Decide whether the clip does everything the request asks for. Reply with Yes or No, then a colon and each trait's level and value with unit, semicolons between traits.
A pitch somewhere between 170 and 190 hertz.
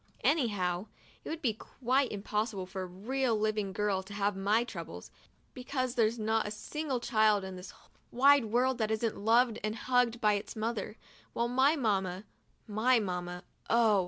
No: high, 220 Hz